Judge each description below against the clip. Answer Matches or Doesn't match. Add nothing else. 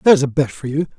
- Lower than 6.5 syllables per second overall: Doesn't match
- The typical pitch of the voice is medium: Matches